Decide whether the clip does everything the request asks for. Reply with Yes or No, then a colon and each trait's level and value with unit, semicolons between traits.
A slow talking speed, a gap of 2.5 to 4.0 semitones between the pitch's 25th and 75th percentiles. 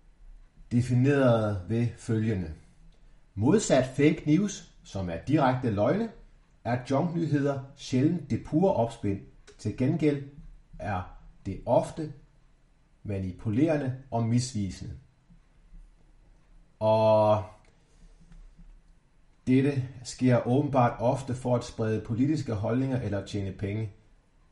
No: slow, 90 wpm; average, 5.2 semitones